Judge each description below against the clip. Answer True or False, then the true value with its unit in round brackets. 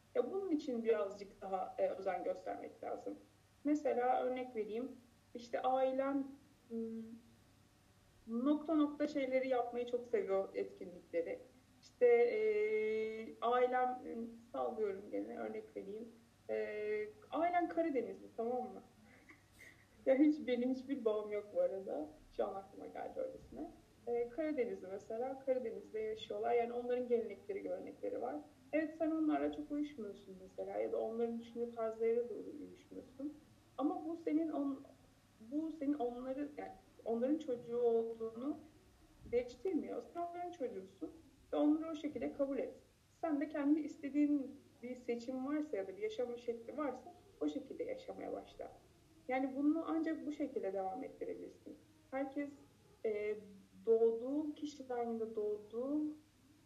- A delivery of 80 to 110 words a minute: False (125 wpm)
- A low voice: False (255 Hz)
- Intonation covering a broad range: False (4.9 semitones)